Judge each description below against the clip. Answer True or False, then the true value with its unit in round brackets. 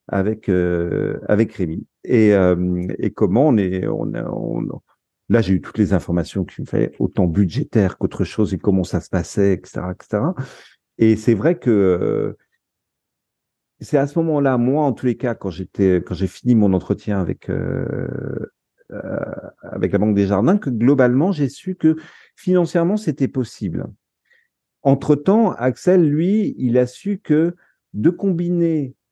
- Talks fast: False (165 wpm)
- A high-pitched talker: False (115 Hz)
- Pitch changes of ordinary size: False (7.6 semitones)